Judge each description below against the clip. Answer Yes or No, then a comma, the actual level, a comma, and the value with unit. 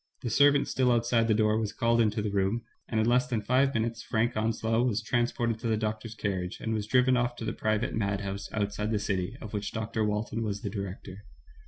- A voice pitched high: No, low, 110 Hz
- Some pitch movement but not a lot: No, narrow, 2.1 semitones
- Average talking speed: No, fast, 225 wpm